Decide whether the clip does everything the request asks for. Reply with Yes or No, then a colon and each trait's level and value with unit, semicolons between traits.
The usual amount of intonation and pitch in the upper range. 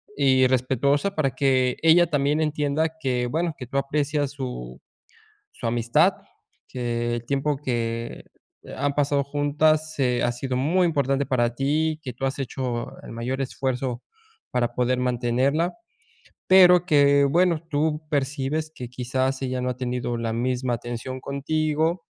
No: average, 3.2 semitones; low, 135 Hz